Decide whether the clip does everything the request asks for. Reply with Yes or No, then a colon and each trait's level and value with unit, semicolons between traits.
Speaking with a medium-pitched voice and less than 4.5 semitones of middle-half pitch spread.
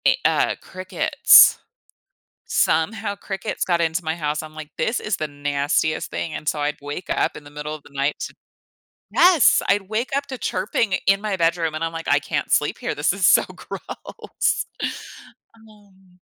No: medium, 170 Hz; average, 4.9 semitones